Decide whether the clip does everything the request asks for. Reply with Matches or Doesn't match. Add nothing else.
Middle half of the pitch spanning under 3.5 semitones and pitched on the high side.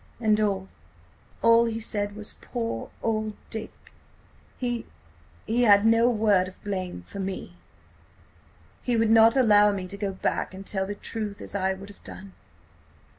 Matches